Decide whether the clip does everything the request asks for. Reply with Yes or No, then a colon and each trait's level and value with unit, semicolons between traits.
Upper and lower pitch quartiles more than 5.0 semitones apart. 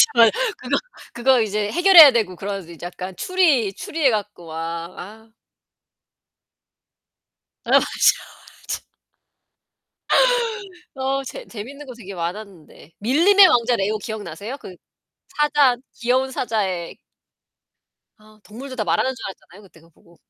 Yes: wide, 5.6 semitones